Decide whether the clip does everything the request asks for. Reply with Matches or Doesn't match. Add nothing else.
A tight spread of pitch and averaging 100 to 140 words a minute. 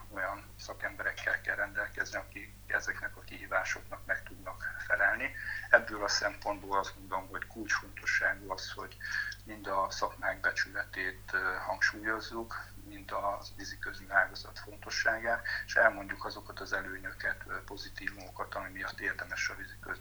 Matches